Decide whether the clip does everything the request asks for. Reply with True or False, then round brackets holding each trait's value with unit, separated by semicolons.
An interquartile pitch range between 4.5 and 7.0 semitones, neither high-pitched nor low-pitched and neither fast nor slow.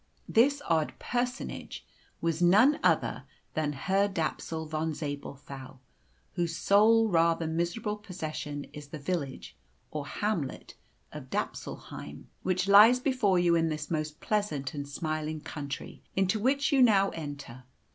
False (5.5 semitones; 165 Hz; 130 wpm)